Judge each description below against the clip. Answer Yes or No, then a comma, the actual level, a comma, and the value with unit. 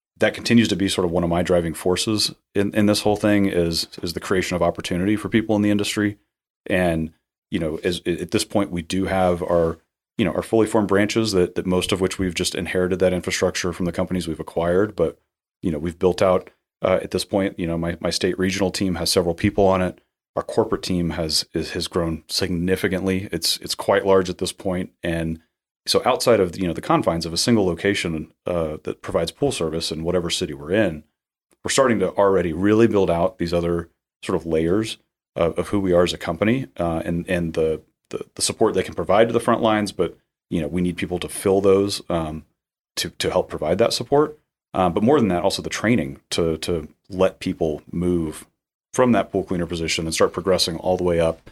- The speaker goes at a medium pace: No, fast, 225 wpm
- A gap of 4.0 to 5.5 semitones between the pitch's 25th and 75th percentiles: No, average, 2.9 semitones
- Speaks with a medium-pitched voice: No, very low, 90 Hz